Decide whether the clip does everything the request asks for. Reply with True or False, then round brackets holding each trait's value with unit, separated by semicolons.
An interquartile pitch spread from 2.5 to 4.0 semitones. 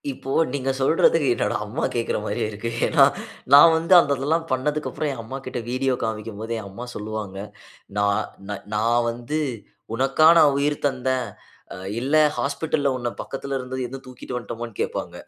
True (3.7 semitones)